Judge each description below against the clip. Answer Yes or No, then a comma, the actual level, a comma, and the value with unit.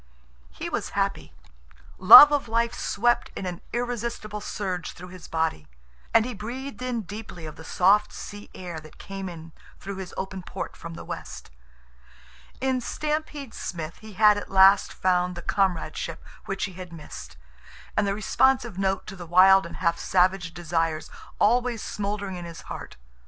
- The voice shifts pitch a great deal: No, average, 3.8 semitones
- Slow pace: No, average, 165 wpm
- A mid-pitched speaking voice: No, high, 195 Hz